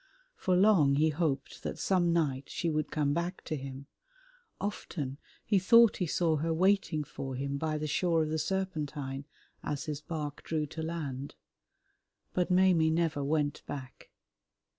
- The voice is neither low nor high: Yes, medium, 155 Hz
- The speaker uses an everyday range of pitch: Yes, average, 3.3 semitones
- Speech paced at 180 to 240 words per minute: No, average, 160 wpm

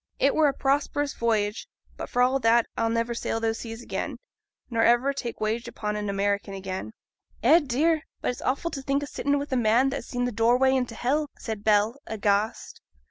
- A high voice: Yes, high, 235 Hz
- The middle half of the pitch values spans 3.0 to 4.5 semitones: Yes, average, 3.7 semitones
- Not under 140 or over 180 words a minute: No, fast, 205 wpm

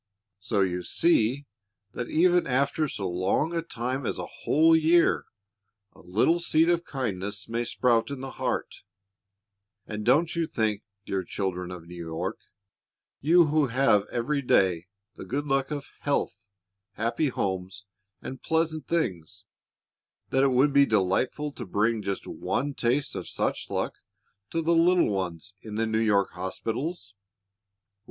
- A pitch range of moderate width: No, wide, 7.1 semitones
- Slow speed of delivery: No, average, 150 wpm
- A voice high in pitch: No, low, 120 Hz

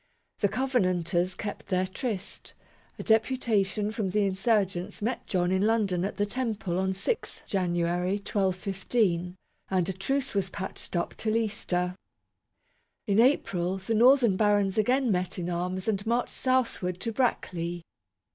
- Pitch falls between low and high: No, high, 195 Hz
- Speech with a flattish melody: No, average, 3.5 semitones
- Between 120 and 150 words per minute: Yes, average, 140 wpm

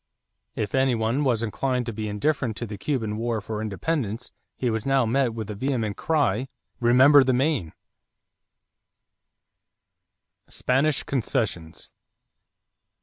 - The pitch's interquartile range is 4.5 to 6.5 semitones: No, average, 3.6 semitones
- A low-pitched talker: Yes, low, 120 Hz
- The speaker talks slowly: Yes, slow, 125 wpm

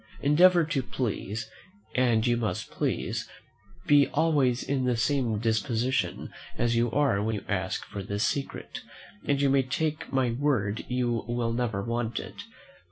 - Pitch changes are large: No, average, 3.6 semitones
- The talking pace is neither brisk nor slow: Yes, average, 155 wpm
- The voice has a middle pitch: No, low, 120 Hz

